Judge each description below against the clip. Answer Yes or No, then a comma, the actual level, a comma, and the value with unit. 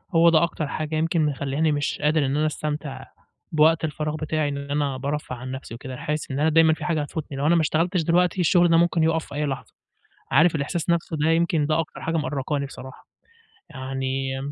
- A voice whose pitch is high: No, medium, 150 Hz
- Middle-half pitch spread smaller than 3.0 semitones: Yes, narrow, 2.6 semitones